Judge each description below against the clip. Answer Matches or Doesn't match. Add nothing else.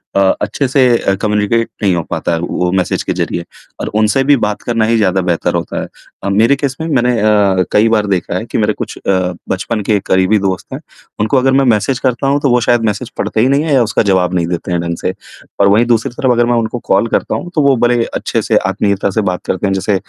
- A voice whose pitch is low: Matches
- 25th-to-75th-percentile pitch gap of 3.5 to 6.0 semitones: Matches